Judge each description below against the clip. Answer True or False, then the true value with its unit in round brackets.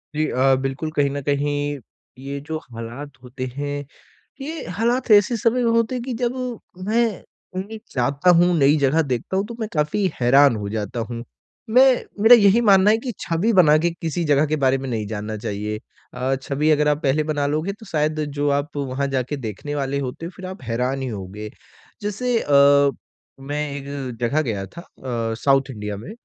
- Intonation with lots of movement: True (5.8 semitones)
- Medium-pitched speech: True (145 Hz)